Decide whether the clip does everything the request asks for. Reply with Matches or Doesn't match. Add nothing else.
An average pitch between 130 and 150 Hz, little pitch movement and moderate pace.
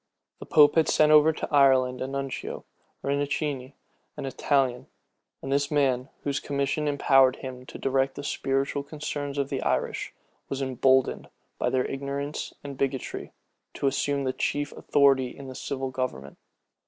Matches